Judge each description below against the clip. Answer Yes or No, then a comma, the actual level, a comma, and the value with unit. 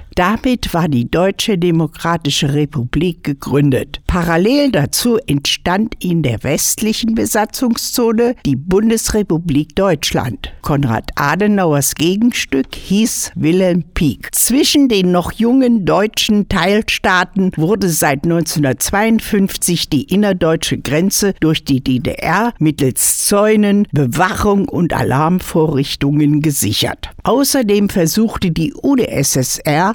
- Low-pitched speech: No, medium, 175 Hz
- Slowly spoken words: Yes, slow, 95 wpm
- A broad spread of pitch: Yes, wide, 6.1 semitones